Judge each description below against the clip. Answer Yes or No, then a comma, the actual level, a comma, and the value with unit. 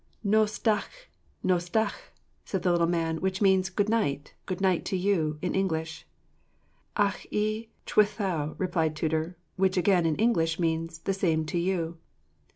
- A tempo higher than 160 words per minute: No, average, 155 wpm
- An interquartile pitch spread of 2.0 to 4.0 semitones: Yes, average, 3.6 semitones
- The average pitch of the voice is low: No, medium, 185 Hz